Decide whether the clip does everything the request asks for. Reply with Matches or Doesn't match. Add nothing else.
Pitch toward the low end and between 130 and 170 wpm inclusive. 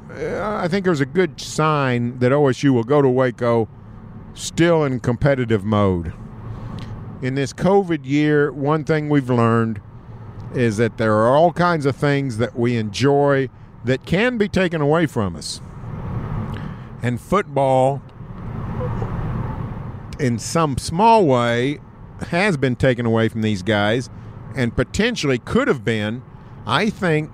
Matches